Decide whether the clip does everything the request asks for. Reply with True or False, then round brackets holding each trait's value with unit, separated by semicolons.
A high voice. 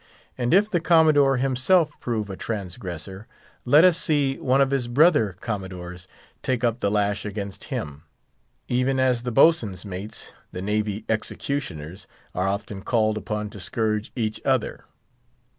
False (110 Hz)